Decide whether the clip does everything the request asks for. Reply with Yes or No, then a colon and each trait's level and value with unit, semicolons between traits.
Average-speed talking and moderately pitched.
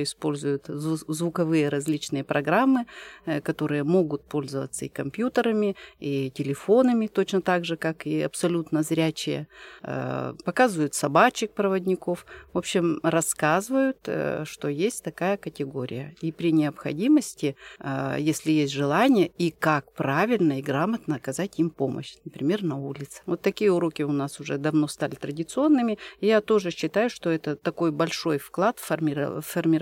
Yes: average, 125 wpm; medium, 160 Hz